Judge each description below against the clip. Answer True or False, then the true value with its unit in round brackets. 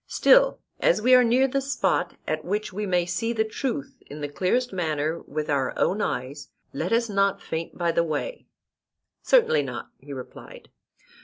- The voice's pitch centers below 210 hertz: True (185 Hz)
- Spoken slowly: False (175 wpm)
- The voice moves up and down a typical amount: False (7.3 semitones)